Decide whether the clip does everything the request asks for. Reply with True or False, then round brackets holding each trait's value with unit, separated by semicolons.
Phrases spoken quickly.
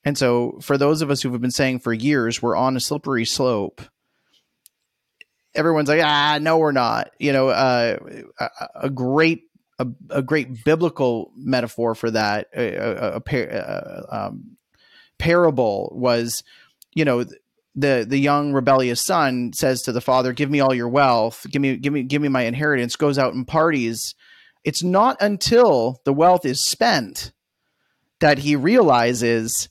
False (165 wpm)